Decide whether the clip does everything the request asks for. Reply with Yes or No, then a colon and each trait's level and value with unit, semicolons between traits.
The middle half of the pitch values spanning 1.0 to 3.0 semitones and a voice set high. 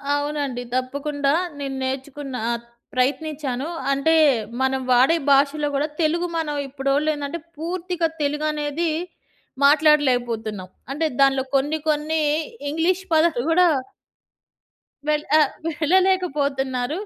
Yes: narrow, 2.6 semitones; very high, 290 Hz